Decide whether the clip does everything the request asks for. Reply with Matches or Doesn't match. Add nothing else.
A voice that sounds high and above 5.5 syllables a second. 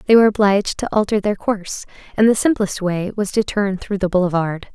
Matches